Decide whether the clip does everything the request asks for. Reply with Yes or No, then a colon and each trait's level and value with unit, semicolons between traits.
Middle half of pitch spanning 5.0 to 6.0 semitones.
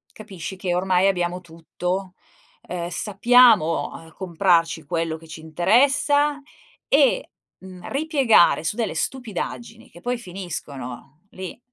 Yes: wide, 5.4 semitones